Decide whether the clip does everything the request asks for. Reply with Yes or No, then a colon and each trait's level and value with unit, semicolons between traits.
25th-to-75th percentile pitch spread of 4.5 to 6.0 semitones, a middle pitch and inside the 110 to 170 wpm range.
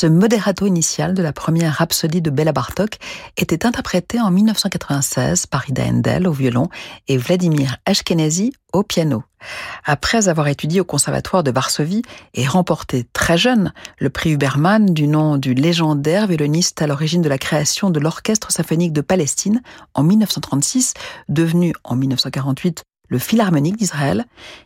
Yes: average, 4.8 semitones; medium, 165 Hz; average, 150 wpm